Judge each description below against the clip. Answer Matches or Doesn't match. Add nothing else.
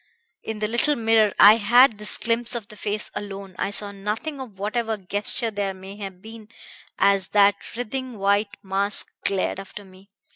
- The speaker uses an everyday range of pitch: Doesn't match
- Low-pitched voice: Doesn't match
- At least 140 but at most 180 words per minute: Matches